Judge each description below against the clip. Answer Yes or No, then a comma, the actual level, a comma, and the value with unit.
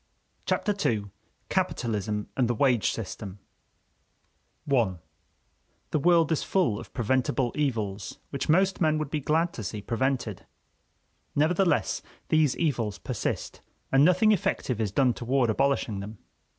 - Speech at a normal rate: No, slow, 130 wpm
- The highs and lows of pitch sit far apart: Yes, wide, 6.1 semitones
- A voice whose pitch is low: Yes, low, 130 Hz